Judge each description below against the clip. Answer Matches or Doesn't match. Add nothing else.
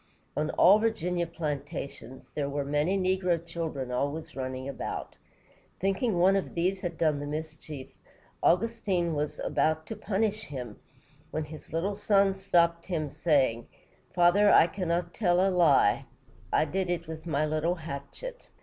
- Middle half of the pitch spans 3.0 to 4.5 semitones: Matches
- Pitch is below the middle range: Doesn't match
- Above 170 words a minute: Doesn't match